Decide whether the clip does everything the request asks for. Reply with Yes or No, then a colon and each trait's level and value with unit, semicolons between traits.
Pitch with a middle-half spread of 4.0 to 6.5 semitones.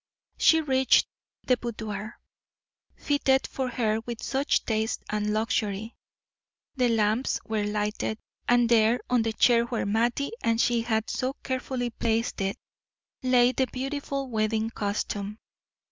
No: average, 2.8 semitones